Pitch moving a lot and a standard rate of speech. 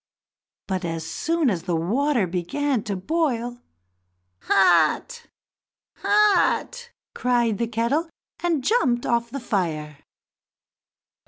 No: wide, 8.3 semitones; slow, 100 wpm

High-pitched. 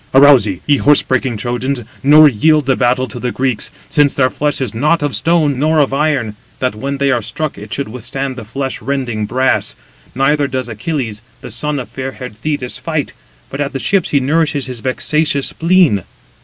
No: low, 135 Hz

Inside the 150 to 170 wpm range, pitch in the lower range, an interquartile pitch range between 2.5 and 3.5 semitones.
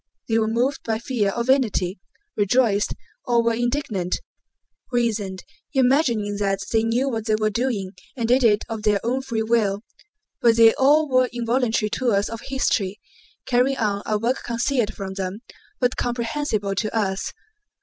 No: average, 160 wpm; high, 230 Hz; average, 3.1 semitones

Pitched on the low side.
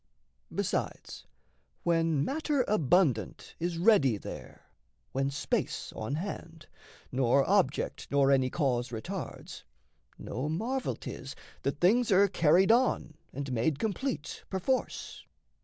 No: medium, 165 Hz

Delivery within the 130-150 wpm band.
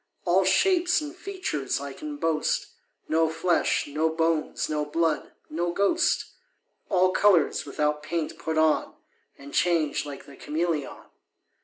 Yes: slow, 135 wpm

